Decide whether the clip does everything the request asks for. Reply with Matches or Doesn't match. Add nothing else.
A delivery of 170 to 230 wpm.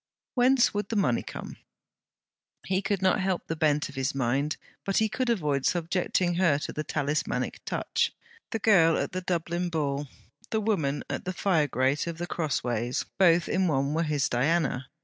Matches